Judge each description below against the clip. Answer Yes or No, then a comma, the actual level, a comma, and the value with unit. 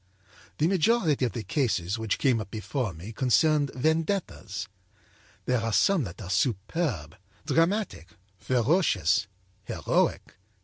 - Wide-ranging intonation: Yes, wide, 7.9 semitones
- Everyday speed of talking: No, slow, 120 wpm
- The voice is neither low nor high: No, low, 125 Hz